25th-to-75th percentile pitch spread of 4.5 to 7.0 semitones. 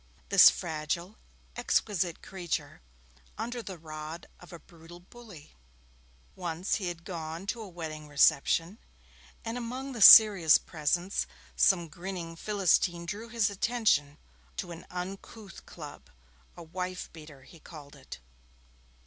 No: average, 3.9 semitones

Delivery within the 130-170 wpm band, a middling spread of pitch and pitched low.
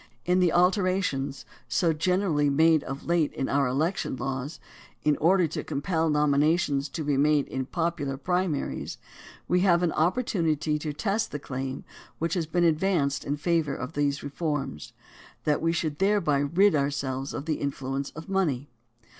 No: average, 165 wpm; average, 3.6 semitones; medium, 150 Hz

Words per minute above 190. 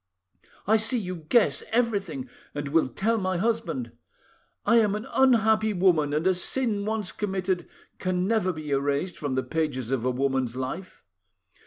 No: average, 160 wpm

